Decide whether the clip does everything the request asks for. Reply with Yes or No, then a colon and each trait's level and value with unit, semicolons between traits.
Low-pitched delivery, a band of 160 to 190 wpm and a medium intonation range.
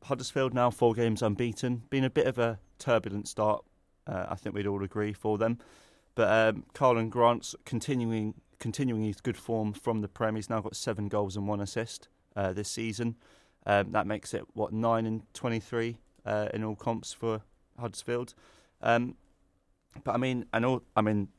No: low, 110 Hz; average, 185 wpm; narrow, 2.2 semitones